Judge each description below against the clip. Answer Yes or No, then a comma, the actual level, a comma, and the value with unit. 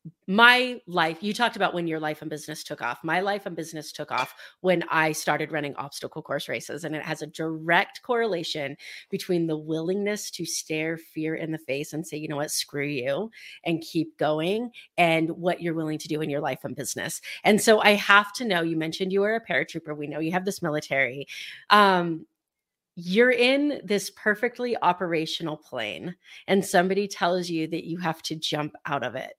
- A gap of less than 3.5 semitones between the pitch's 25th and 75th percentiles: No, average, 4.2 semitones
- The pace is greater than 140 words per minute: Yes, average, 200 wpm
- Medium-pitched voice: Yes, medium, 165 Hz